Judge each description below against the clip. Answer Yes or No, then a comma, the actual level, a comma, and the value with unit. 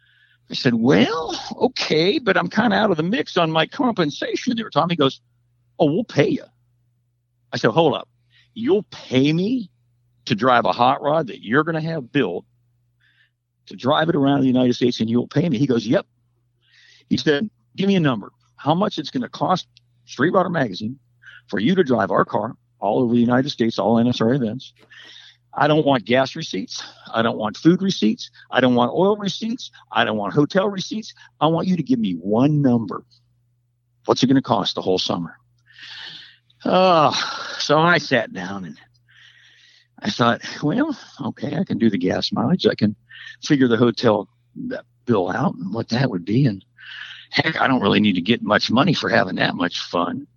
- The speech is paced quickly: No, average, 195 wpm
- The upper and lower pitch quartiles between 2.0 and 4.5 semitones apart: No, average, 5.0 semitones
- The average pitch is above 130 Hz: No, low, 125 Hz